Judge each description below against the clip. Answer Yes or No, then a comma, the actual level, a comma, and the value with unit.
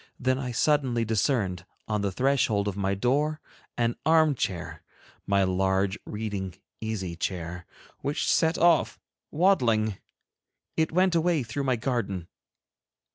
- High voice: No, low, 115 Hz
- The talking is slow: Yes, slow, 125 wpm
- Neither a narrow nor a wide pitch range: No, wide, 6.6 semitones